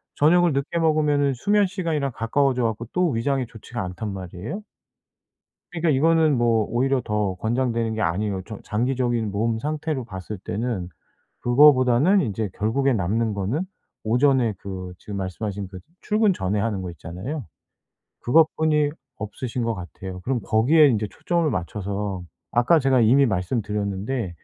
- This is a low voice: Yes, low, 115 Hz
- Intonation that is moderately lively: No, wide, 5.7 semitones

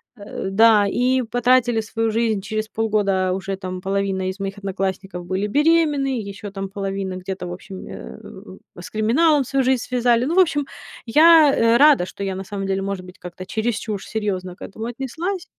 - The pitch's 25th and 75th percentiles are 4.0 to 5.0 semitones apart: Yes, average, 4.3 semitones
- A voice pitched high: Yes, high, 210 Hz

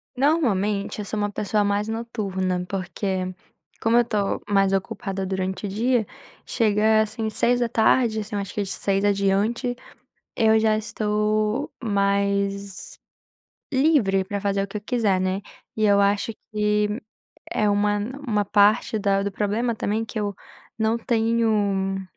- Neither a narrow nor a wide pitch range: No, narrow, 1.9 semitones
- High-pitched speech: Yes, high, 210 Hz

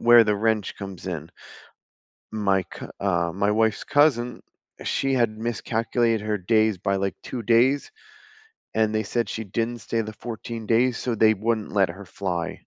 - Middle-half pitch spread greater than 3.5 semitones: No, average, 2.8 semitones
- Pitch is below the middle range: Yes, low, 110 Hz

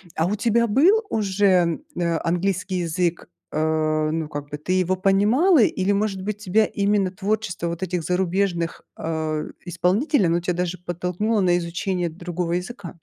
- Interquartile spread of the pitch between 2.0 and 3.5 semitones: Yes, average, 3.1 semitones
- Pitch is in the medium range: Yes, medium, 180 Hz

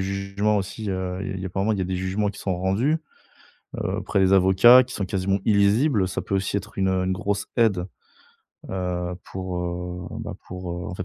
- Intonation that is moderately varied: No, narrow, 1.6 semitones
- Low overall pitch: Yes, very low, 95 Hz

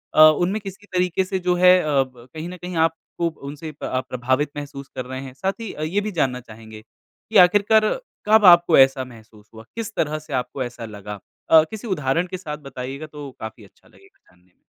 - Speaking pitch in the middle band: Yes, medium, 150 Hz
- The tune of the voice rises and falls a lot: Yes, wide, 6.2 semitones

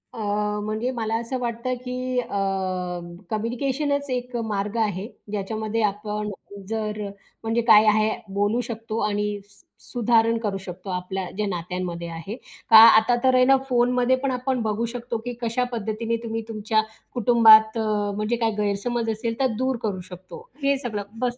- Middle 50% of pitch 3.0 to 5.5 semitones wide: No, narrow, 2.6 semitones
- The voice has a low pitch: No, high, 225 Hz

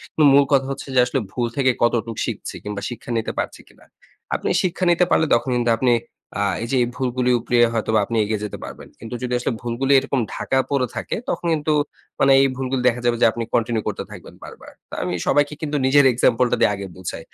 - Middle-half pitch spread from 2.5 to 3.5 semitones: Yes, average, 2.8 semitones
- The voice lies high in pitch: No, low, 125 Hz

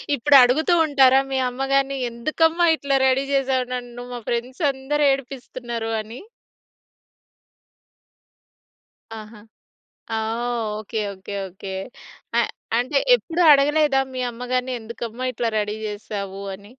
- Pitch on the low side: No, very high, 250 Hz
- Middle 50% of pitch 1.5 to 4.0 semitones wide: Yes, average, 3.2 semitones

